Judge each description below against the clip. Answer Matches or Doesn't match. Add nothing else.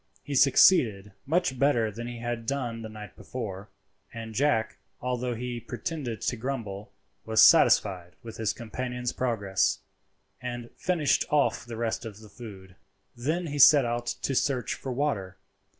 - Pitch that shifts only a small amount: Doesn't match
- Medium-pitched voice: Doesn't match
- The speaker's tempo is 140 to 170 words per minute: Matches